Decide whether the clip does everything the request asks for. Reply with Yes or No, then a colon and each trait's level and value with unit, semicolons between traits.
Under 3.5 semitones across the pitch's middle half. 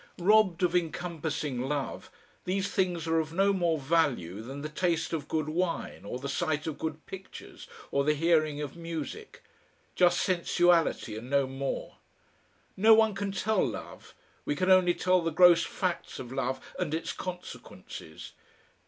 No: average, 3.8 semitones